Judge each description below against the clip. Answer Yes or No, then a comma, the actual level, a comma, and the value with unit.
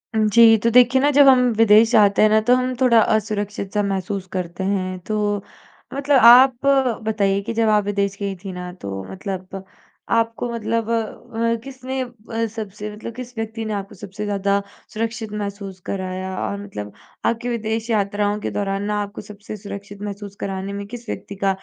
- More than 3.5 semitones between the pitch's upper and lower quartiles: No, narrow, 2.5 semitones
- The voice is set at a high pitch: Yes, high, 210 Hz